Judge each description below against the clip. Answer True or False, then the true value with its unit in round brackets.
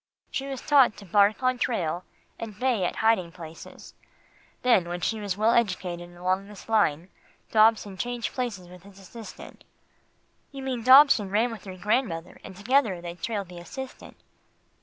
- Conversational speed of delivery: True (160 wpm)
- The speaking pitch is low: False (210 Hz)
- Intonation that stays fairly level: False (4.9 semitones)